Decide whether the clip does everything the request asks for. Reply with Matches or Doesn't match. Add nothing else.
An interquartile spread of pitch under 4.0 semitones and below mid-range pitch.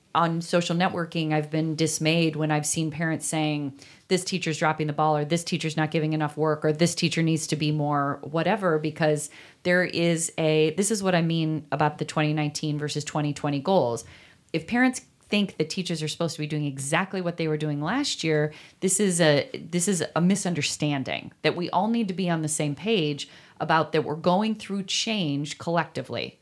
Doesn't match